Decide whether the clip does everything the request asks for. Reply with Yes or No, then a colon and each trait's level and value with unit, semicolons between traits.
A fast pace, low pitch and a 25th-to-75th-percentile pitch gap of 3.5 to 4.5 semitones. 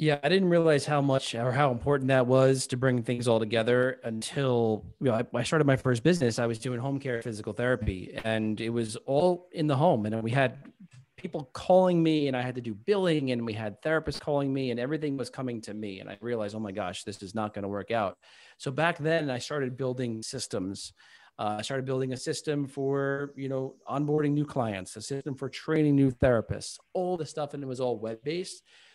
Yes: fast, 225 wpm; low, 130 Hz; average, 4.2 semitones